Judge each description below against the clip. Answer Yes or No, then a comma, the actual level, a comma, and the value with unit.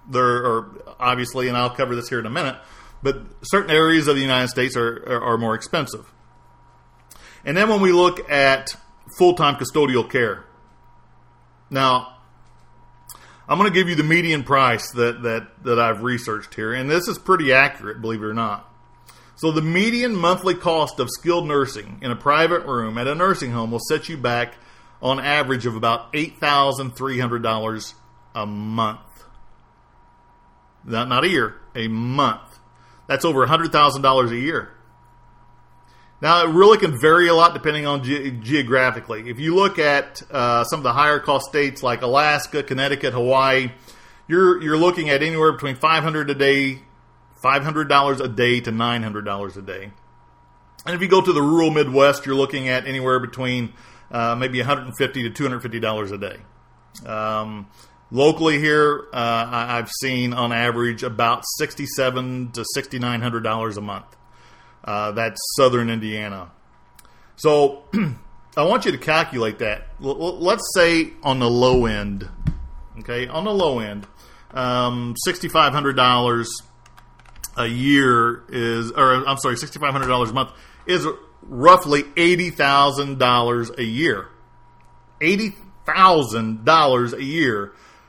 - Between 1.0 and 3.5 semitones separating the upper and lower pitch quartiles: No, average, 3.9 semitones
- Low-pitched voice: Yes, low, 125 Hz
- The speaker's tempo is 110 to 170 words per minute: Yes, average, 160 wpm